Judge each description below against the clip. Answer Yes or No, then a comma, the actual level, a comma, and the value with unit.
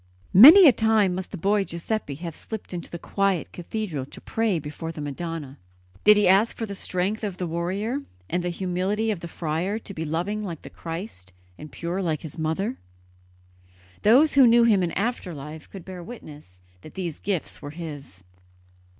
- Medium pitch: Yes, medium, 180 Hz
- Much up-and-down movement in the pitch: No, average, 4.6 semitones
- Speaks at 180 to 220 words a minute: Yes, average, 185 wpm